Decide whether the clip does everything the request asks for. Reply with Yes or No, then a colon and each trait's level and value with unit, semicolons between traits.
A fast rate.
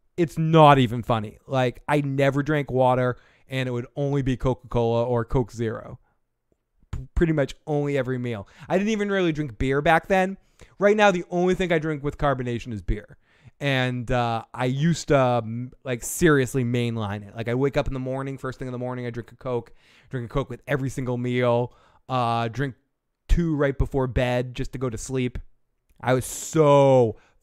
No: average, 195 wpm